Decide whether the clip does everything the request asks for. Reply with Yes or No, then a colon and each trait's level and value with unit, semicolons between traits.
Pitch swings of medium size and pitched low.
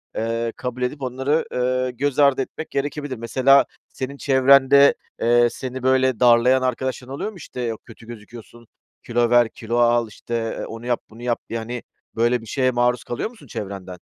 No: narrow, 2.1 semitones; low, 125 Hz